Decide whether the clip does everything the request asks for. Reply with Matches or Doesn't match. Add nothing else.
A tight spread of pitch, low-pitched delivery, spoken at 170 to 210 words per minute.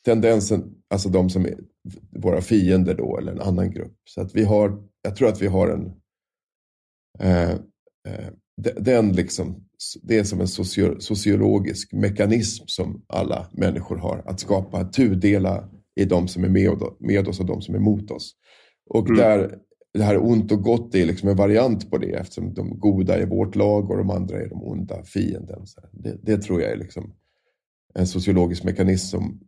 Matches